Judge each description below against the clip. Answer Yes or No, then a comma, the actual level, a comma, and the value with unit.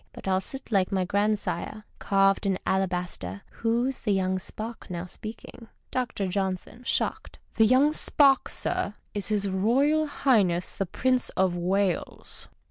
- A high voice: Yes, high, 200 Hz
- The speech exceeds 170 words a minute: No, average, 150 wpm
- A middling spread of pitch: Yes, average, 4.0 semitones